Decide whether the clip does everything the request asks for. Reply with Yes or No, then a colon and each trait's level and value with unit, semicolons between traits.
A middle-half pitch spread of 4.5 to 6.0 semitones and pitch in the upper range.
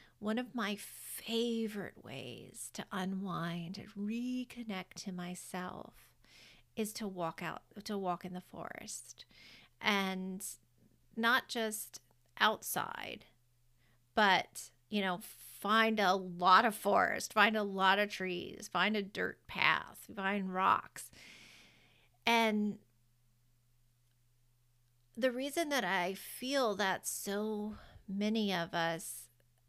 No: average, 3.9 semitones; high, 195 Hz